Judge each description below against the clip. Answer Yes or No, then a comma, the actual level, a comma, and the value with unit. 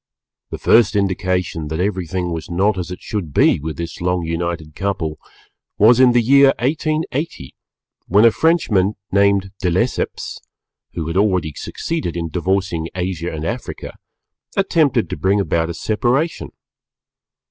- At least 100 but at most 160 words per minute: Yes, average, 145 wpm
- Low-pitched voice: Yes, very low, 95 Hz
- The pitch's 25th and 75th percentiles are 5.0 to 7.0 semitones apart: Yes, wide, 5.5 semitones